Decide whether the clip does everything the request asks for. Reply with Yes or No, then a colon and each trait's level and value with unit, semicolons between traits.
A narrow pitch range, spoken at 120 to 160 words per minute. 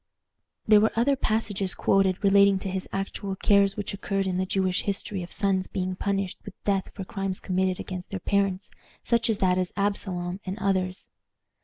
No: narrow, 1.3 semitones; average, 175 wpm